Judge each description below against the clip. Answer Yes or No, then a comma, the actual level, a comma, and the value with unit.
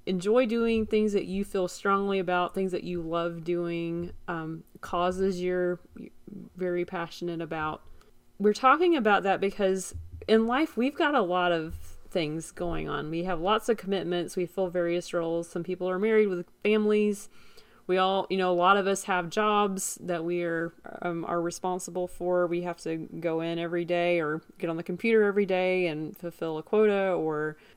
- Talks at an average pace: Yes, average, 185 wpm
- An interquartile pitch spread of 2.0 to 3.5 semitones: Yes, narrow, 2.6 semitones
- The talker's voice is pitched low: No, medium, 180 Hz